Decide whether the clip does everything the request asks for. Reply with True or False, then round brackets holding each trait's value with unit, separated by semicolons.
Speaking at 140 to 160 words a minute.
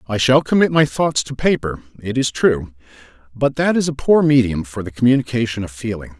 False (205 wpm)